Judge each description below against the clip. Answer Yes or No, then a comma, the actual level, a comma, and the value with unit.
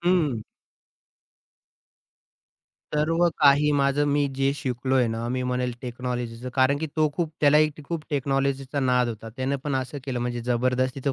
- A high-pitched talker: No, low, 135 Hz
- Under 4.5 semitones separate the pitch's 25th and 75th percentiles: Yes, average, 2.7 semitones